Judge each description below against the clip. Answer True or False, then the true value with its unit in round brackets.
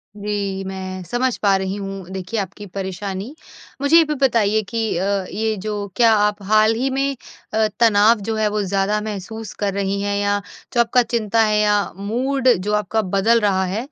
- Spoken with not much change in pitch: True (2.3 semitones)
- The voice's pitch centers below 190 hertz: False (210 Hz)